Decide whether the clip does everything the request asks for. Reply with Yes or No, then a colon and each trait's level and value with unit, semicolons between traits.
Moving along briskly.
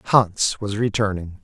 No: slow, 125 wpm